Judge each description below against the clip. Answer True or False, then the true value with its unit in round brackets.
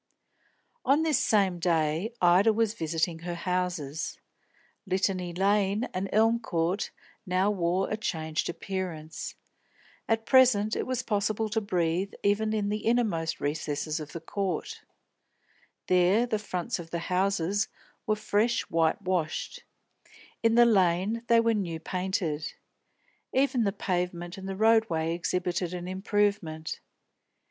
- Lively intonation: False (4.1 semitones)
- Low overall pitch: False (190 Hz)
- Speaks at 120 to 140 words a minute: True (135 wpm)